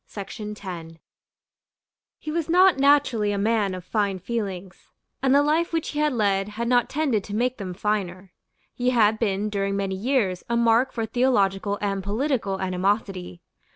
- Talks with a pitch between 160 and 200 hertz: No, high, 210 Hz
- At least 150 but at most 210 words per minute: Yes, average, 155 wpm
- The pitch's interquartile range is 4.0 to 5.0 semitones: Yes, average, 4.5 semitones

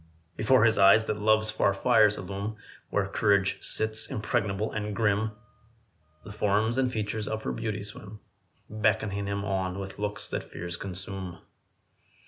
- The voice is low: Yes, low, 105 Hz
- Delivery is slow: No, average, 145 wpm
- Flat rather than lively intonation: Yes, narrow, 1.8 semitones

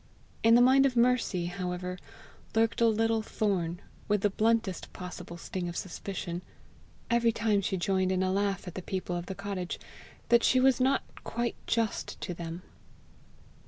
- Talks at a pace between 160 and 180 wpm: Yes, average, 165 wpm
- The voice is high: Yes, high, 195 Hz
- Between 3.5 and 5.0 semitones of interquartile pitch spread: Yes, average, 4.1 semitones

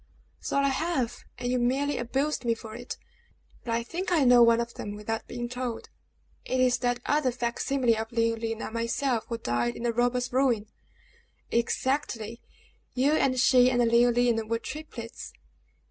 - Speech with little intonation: Yes, narrow, 1.9 semitones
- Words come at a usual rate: Yes, average, 170 wpm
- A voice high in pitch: Yes, high, 240 Hz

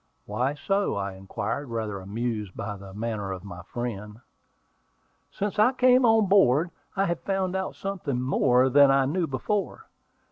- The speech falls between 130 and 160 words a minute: Yes, average, 155 wpm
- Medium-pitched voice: No, low, 130 Hz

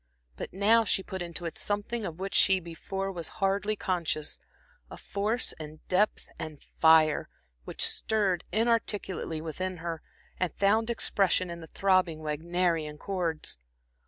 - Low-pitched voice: No, medium, 185 Hz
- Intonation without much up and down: No, average, 3.5 semitones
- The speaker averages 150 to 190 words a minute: No, average, 140 wpm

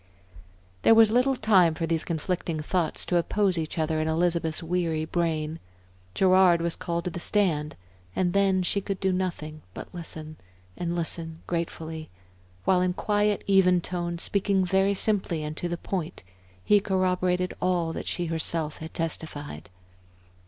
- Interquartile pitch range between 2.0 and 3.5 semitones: Yes, narrow, 2.5 semitones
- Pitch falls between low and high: Yes, medium, 175 Hz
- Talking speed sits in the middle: Yes, average, 155 wpm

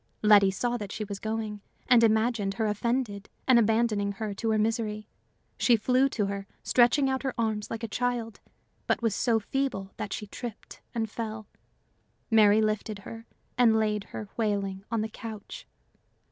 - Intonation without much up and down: Yes, narrow, 2.0 semitones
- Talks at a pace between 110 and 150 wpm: No, average, 170 wpm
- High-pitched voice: Yes, high, 220 Hz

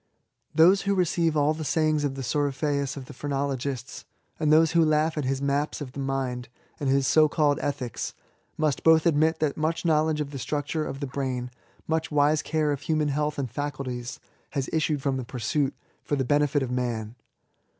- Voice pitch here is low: No, medium, 145 Hz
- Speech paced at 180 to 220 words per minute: Yes, average, 190 wpm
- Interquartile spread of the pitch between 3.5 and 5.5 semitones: No, narrow, 2.4 semitones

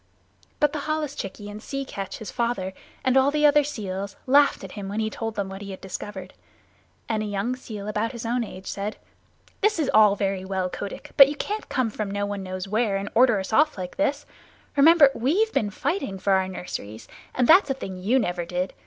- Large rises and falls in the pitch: Yes, wide, 5.9 semitones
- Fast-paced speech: Yes, fast, 215 wpm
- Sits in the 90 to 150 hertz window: No, high, 215 Hz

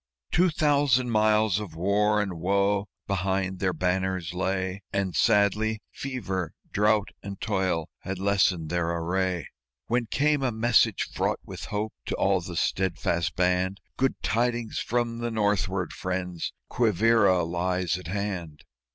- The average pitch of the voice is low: Yes, very low, 95 Hz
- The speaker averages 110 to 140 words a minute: Yes, slow, 135 wpm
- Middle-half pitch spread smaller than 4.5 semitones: Yes, average, 3.2 semitones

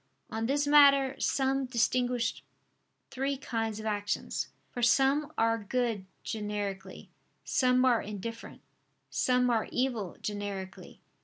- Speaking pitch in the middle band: No, high, 235 Hz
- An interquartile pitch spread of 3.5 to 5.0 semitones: Yes, average, 3.9 semitones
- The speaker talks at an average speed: No, slow, 110 wpm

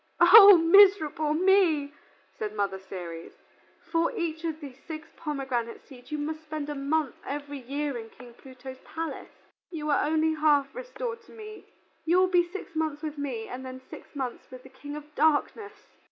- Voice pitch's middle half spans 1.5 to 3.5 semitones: No, average, 4.0 semitones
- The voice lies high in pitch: Yes, very high, 300 Hz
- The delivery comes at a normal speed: Yes, average, 175 wpm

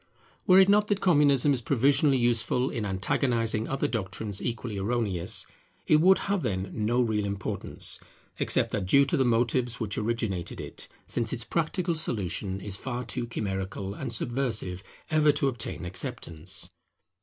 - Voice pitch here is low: Yes, low, 115 Hz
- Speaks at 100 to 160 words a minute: Yes, average, 155 wpm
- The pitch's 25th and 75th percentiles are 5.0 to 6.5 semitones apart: Yes, average, 5.3 semitones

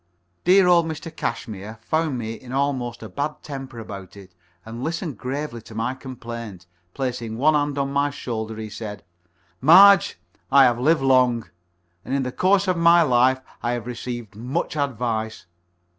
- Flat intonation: No, average, 4.3 semitones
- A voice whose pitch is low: Yes, low, 125 Hz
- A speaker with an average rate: Yes, average, 165 wpm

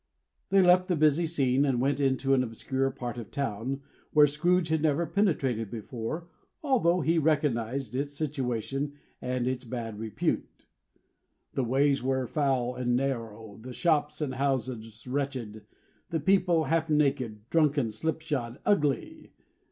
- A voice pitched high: No, low, 135 Hz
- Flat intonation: No, average, 4.0 semitones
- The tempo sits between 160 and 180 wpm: No, average, 145 wpm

